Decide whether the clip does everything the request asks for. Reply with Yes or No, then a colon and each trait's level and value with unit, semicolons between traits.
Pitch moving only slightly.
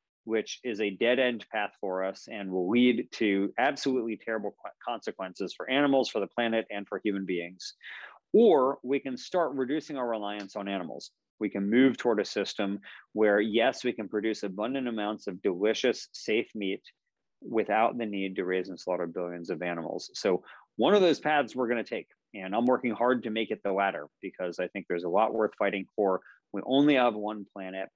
No: average, 3.9 semitones